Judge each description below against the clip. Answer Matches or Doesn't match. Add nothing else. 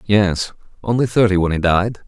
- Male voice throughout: Matches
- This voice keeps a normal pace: Matches